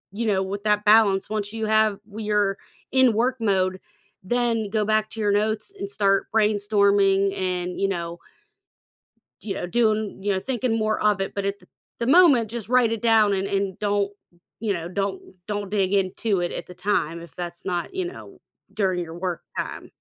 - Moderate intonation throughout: No, narrow, 2.2 semitones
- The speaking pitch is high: Yes, high, 205 Hz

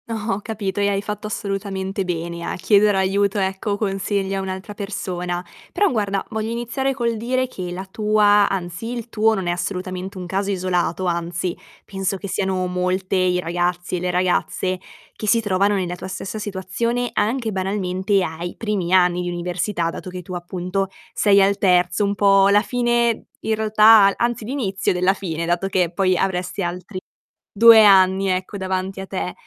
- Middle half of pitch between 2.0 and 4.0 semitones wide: Yes, narrow, 2.4 semitones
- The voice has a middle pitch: No, high, 195 Hz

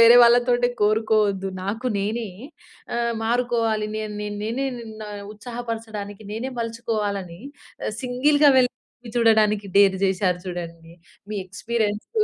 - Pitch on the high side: Yes, high, 220 Hz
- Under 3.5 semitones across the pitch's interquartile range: Yes, average, 2.9 semitones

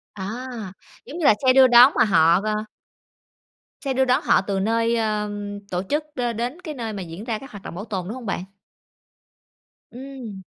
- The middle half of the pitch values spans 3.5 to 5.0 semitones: Yes, average, 4.2 semitones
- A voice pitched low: No, high, 220 Hz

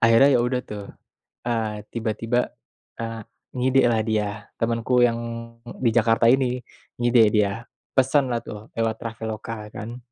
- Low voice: Yes, low, 115 Hz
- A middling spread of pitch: No, narrow, 1.8 semitones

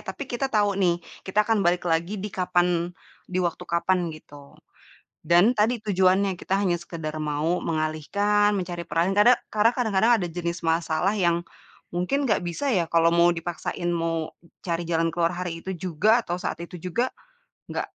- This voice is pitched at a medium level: Yes, medium, 175 Hz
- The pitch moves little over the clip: No, average, 3.3 semitones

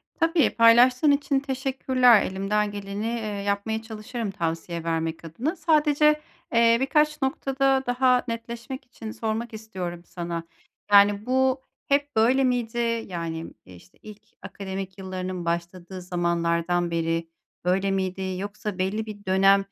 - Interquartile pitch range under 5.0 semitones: No, wide, 5.6 semitones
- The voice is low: No, high, 210 Hz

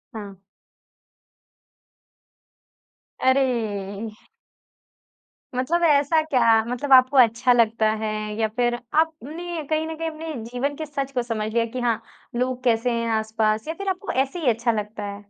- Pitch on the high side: Yes, very high, 250 Hz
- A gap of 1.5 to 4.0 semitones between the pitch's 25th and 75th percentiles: No, average, 5.3 semitones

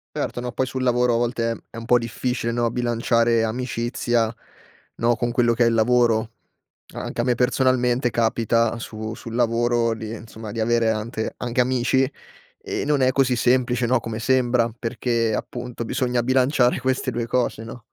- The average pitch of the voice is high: No, low, 120 Hz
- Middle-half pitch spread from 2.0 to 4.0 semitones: No, narrow, 1.3 semitones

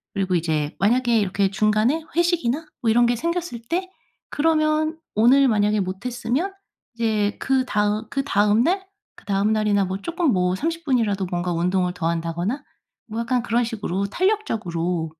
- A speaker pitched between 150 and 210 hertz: No, high, 220 Hz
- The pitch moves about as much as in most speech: No, wide, 6.1 semitones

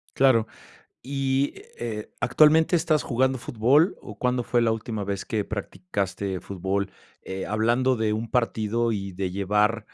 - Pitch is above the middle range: No, low, 115 Hz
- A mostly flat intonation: No, average, 4.3 semitones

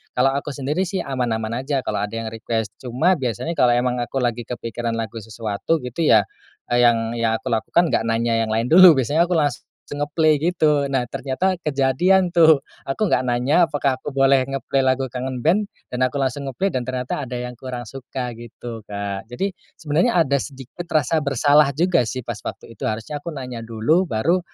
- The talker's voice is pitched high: No, low, 130 Hz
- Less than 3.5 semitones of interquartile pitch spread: No, average, 4.2 semitones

